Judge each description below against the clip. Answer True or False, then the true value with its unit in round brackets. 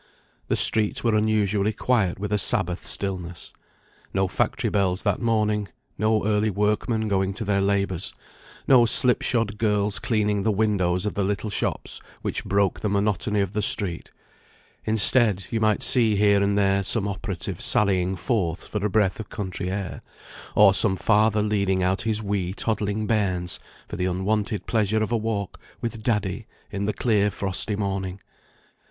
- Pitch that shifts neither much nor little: False (1.9 semitones)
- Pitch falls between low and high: False (105 Hz)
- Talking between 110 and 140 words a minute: False (165 wpm)